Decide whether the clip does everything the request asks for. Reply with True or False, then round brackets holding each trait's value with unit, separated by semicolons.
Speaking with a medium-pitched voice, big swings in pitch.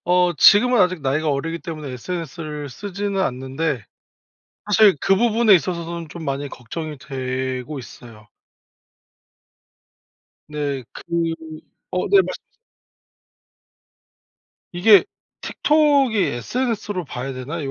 True (165 Hz; 6.6 semitones)